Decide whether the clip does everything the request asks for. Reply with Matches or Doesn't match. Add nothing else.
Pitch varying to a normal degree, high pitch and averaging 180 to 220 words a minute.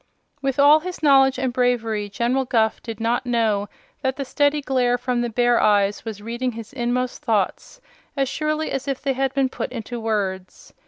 Matches